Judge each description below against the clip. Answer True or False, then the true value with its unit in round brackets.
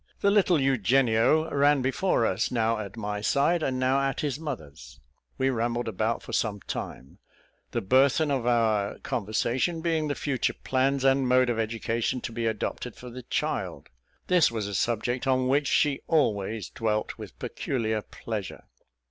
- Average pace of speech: True (165 wpm)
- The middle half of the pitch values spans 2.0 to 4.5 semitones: True (3.8 semitones)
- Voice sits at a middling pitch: False (125 Hz)